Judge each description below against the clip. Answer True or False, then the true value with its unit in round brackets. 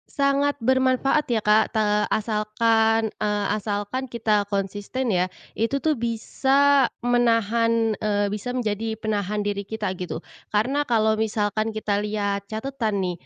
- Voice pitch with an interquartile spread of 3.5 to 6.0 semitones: False (2.8 semitones)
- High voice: True (220 Hz)